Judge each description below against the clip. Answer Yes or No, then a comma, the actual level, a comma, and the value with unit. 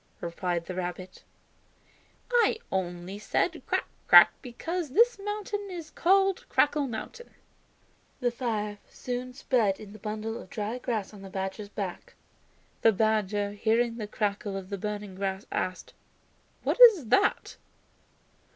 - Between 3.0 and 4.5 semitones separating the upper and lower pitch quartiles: No, average, 5.2 semitones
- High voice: Yes, high, 215 Hz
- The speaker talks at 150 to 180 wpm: No, slow, 135 wpm